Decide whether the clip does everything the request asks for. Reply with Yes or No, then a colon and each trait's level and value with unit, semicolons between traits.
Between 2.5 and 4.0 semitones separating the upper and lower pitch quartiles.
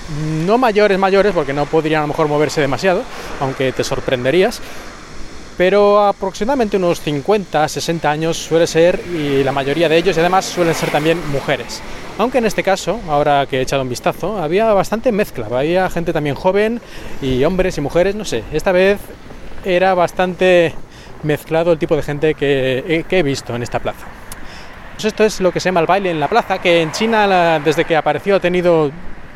No: average, 4.5 semitones